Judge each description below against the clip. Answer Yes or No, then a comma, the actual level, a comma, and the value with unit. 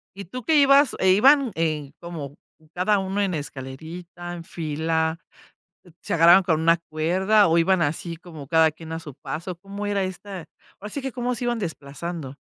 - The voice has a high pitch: No, medium, 170 Hz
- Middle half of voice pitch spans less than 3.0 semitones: No, average, 3.8 semitones